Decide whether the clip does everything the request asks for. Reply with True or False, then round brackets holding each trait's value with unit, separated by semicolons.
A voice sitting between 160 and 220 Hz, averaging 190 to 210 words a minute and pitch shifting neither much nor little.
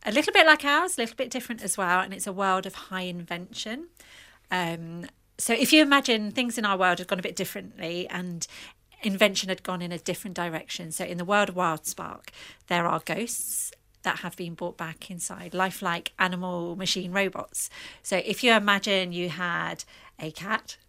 True (190 Hz; 195 wpm; 3.8 semitones)